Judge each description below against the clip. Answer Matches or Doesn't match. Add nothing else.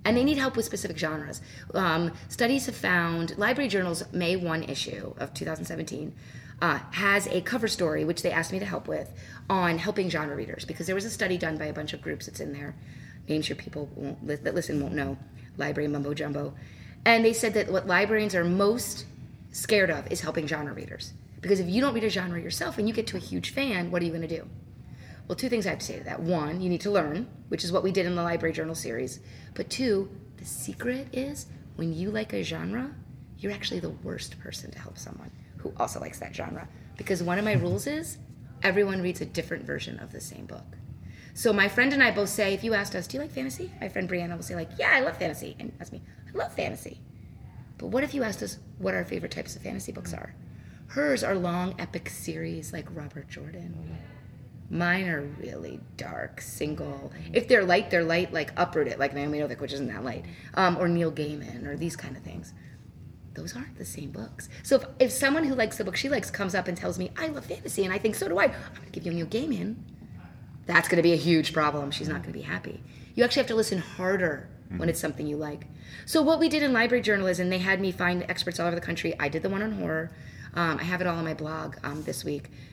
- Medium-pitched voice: Matches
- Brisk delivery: Matches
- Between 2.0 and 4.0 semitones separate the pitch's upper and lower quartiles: Doesn't match